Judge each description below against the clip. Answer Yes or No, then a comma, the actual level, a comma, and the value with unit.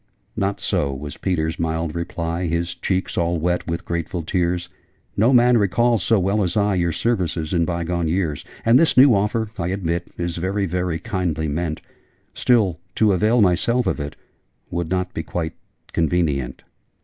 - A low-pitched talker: Yes, very low, 90 Hz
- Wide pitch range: No, average, 3.0 semitones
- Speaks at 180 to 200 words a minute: No, average, 165 wpm